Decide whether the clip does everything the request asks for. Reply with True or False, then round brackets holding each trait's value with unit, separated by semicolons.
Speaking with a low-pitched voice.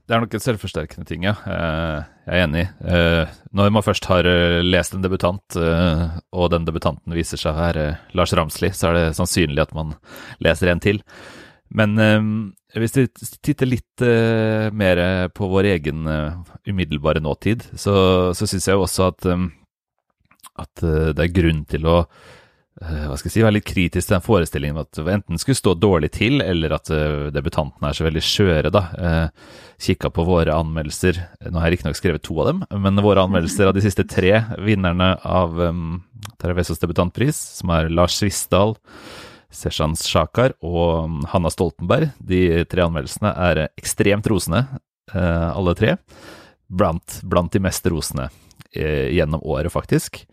True (90 Hz)